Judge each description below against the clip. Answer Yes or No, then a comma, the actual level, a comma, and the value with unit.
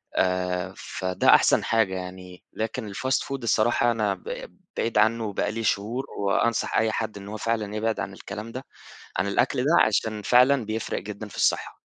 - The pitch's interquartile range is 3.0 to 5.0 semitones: No, narrow, 2.5 semitones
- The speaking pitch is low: Yes, low, 110 Hz